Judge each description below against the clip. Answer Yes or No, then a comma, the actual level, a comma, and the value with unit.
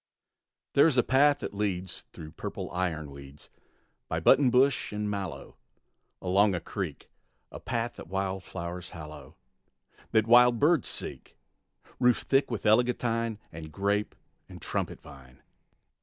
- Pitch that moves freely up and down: Yes, wide, 6.1 semitones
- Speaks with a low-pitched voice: Yes, low, 100 Hz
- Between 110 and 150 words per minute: Yes, slow, 135 wpm